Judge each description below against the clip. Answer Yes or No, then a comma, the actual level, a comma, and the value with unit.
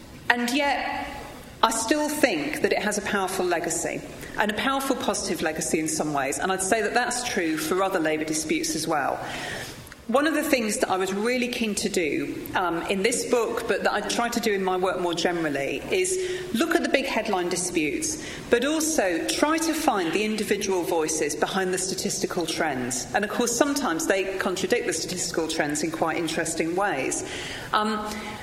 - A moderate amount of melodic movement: No, wide, 7.3 semitones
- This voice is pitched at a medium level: No, high, 210 Hz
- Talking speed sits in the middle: Yes, average, 190 wpm